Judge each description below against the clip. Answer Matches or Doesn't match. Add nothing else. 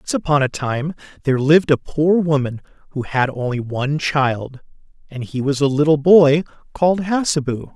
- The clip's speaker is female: Doesn't match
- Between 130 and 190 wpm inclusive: Matches